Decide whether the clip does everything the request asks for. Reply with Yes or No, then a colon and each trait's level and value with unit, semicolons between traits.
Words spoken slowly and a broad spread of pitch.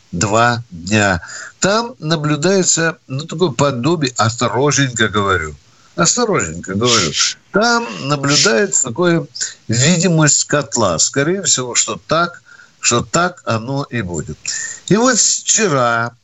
Yes: slow, 105 wpm; wide, 6.8 semitones